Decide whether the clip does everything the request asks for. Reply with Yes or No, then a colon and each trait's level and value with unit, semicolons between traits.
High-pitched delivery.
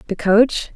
Yes: high, 215 Hz